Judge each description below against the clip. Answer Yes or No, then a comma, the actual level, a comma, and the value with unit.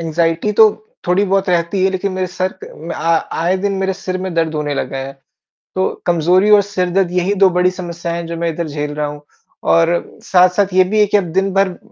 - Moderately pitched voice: Yes, medium, 180 Hz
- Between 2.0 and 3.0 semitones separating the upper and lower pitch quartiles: Yes, narrow, 2.4 semitones